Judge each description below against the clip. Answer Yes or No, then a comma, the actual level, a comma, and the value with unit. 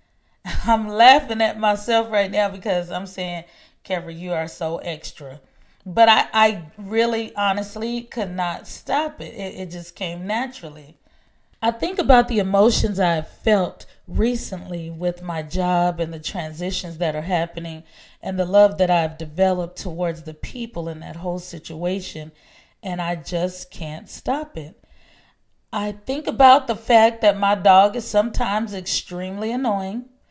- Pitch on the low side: No, high, 190 Hz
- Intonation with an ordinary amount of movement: Yes, average, 4.3 semitones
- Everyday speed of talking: Yes, average, 150 wpm